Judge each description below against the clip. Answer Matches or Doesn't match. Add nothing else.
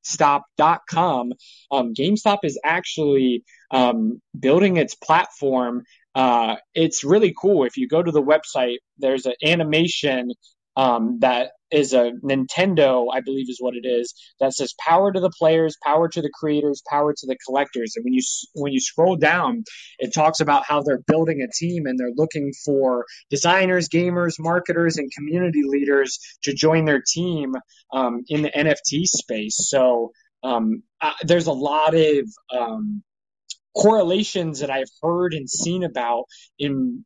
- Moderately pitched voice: Matches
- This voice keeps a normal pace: Matches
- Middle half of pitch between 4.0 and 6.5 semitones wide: Matches